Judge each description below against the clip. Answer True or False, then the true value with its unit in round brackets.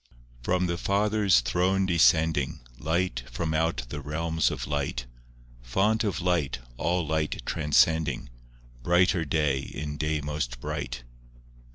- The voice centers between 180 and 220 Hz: False (80 Hz)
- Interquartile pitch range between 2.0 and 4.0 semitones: True (3.5 semitones)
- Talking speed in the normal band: False (130 wpm)